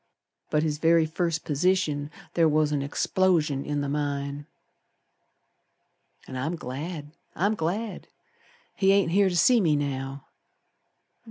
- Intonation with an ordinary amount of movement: Yes, average, 3.7 semitones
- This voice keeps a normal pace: No, slow, 125 wpm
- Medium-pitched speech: Yes, medium, 155 Hz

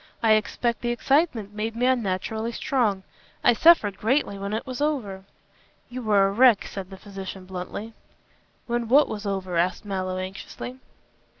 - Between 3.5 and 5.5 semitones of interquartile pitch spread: Yes, average, 3.8 semitones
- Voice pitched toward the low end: No, high, 215 Hz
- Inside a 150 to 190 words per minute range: Yes, average, 160 wpm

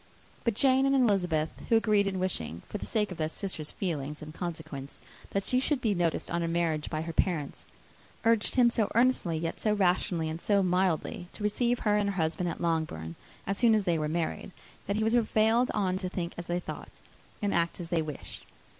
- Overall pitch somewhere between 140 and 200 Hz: Yes, medium, 185 Hz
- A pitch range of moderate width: Yes, average, 4.5 semitones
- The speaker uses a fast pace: Yes, fast, 215 wpm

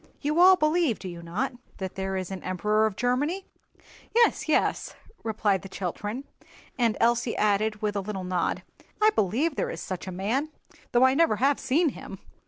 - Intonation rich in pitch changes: Yes, wide, 6.6 semitones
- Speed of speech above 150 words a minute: Yes, average, 185 wpm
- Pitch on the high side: Yes, high, 220 Hz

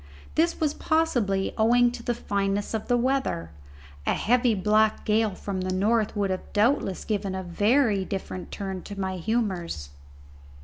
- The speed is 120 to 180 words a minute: Yes, average, 160 wpm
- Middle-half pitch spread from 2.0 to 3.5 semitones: No, average, 3.9 semitones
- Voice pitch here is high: Yes, high, 210 Hz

